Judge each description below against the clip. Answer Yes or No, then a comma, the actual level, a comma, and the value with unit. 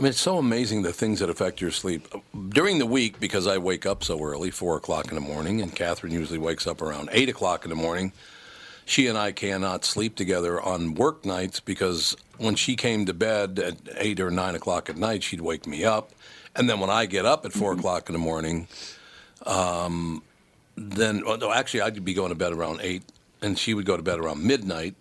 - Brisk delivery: Yes, fast, 225 wpm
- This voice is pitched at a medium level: No, very low, 95 Hz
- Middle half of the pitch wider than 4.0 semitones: Yes, average, 4.5 semitones